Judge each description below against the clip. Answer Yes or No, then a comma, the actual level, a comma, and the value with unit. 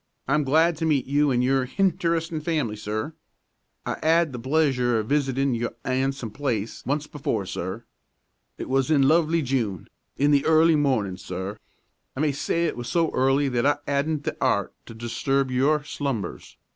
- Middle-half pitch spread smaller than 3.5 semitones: No, average, 3.9 semitones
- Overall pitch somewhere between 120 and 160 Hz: Yes, low, 135 Hz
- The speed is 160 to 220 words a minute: Yes, average, 170 wpm